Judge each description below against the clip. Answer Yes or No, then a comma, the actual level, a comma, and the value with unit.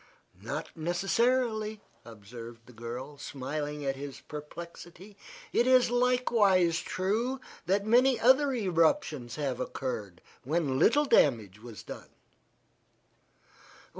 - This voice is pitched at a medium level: Yes, medium, 165 Hz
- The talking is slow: Yes, slow, 105 wpm